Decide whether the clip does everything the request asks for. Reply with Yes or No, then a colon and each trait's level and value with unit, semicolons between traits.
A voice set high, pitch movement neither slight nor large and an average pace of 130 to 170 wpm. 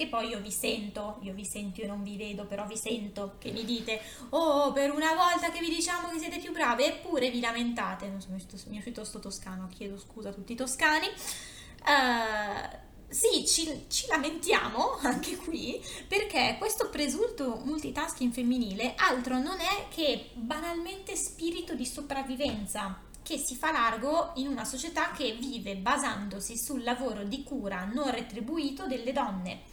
No: very high, 255 Hz; wide, 6.4 semitones; average, 165 wpm